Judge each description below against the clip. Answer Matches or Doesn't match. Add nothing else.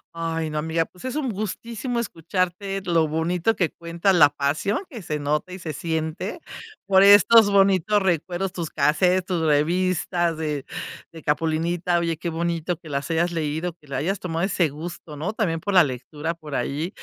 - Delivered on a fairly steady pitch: Doesn't match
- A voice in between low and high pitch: Matches